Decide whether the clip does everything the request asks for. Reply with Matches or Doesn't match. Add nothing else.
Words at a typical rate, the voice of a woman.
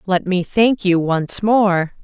Matches